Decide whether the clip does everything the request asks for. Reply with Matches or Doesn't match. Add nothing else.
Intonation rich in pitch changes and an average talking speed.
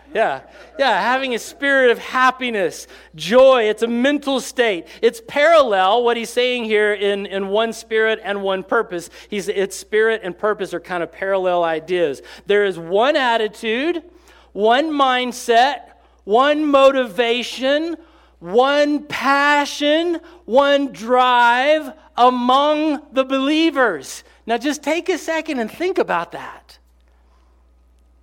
Doesn't match